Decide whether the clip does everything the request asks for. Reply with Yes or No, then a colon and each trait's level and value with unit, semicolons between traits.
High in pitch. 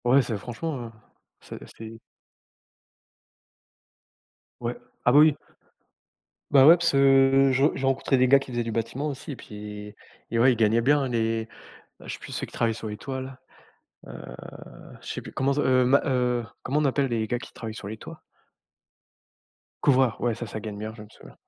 No: low, 125 Hz